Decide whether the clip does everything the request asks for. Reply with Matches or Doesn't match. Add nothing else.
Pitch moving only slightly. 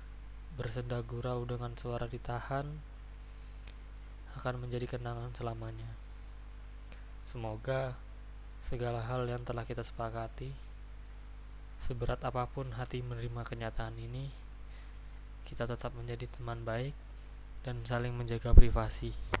Matches